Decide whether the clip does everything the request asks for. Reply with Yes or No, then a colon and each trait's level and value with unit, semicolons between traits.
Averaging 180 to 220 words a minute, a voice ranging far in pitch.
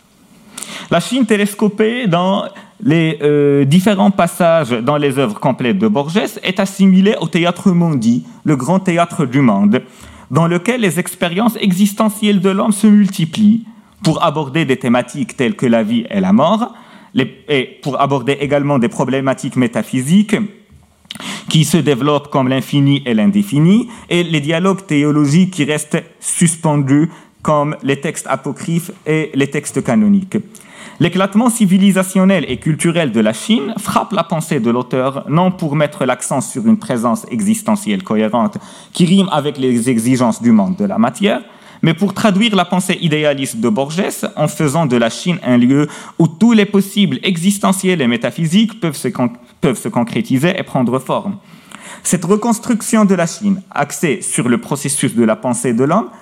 No: average, 160 wpm; wide, 5.9 semitones